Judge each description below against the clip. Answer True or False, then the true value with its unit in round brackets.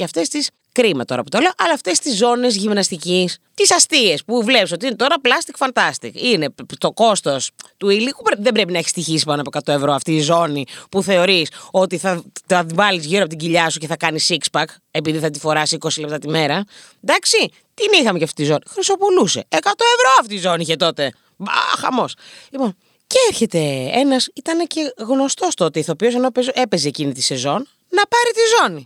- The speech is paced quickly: True (200 wpm)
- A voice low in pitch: False (190 Hz)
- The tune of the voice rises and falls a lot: True (8.7 semitones)